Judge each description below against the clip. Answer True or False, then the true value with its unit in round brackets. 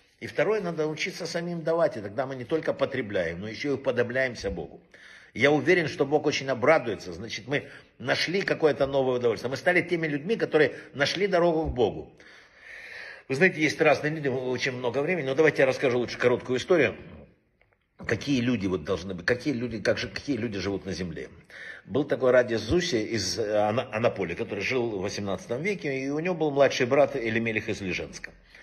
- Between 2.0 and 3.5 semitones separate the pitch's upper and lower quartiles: False (5.1 semitones)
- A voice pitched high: False (135 Hz)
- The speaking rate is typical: False (180 wpm)